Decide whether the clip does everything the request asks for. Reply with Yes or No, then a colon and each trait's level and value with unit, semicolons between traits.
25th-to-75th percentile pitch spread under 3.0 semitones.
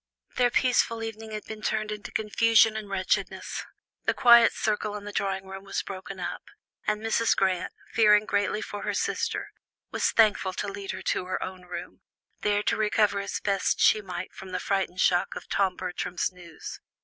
Yes: narrow, 2.4 semitones